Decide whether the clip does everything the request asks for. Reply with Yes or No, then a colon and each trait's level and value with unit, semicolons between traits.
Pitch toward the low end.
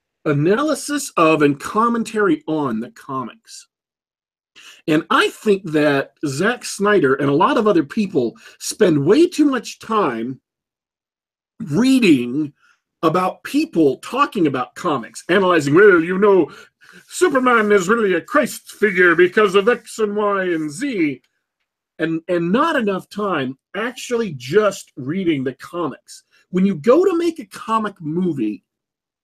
No: high, 210 Hz